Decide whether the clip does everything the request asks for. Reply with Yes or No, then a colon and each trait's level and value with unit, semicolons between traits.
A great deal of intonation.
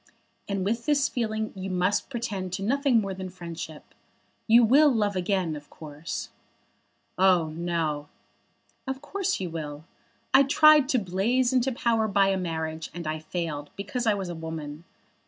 Yes: wide, 6.2 semitones